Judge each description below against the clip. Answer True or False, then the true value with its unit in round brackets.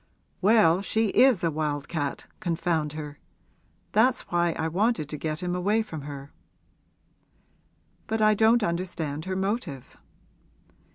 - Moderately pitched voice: True (175 Hz)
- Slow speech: True (130 wpm)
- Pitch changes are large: True (5.7 semitones)